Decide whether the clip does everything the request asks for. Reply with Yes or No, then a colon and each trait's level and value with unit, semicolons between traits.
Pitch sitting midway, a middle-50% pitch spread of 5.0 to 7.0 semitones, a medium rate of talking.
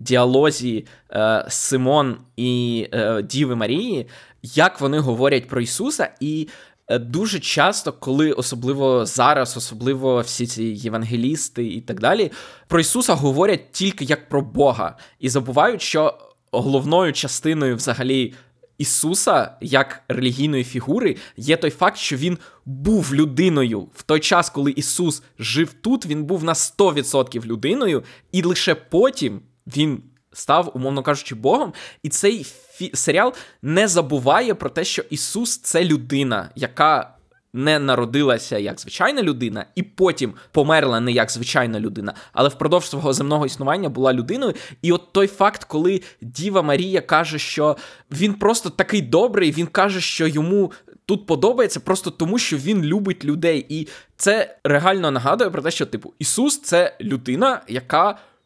Yes: medium, 150 Hz; average, 5.3 semitones; average, 145 wpm